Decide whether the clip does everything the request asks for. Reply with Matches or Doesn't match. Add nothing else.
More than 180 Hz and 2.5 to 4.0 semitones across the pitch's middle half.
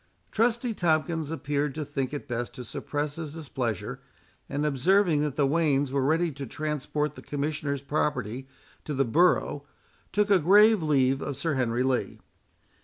Doesn't match